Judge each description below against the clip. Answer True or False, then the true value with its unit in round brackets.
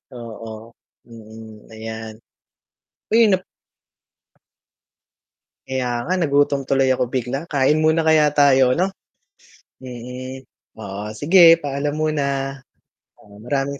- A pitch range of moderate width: True (4.1 semitones)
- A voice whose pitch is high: False (135 Hz)